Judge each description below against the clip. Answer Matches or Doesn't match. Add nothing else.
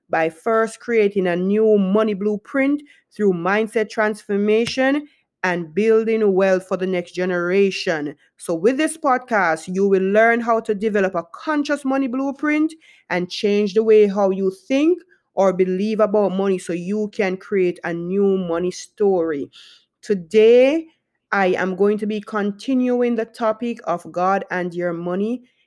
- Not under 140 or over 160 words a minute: Matches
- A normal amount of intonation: Matches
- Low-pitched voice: Doesn't match